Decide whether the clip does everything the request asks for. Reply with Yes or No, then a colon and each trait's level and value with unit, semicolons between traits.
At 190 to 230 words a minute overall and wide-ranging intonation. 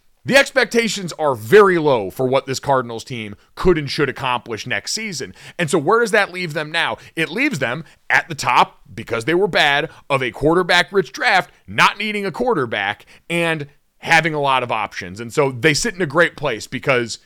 Yes: average, 200 wpm; wide, 6.1 semitones